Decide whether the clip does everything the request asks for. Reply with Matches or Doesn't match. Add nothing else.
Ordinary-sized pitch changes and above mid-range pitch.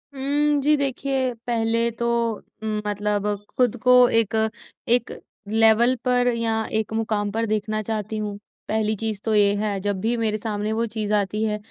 Doesn't match